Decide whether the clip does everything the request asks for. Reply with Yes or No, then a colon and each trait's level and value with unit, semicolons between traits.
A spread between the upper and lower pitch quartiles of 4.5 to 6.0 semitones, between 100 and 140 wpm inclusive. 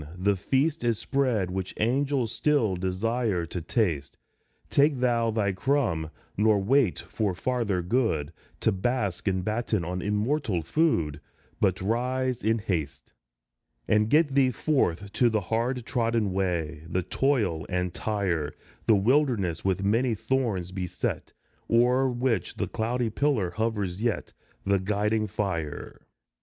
Yes: average, 5.1 semitones; slow, 135 wpm